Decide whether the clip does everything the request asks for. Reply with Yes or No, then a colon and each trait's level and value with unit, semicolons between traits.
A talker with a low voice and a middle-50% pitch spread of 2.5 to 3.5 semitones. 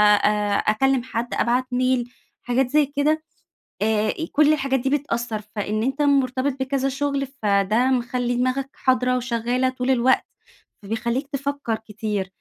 No: very high, 255 Hz; average, 2.8 semitones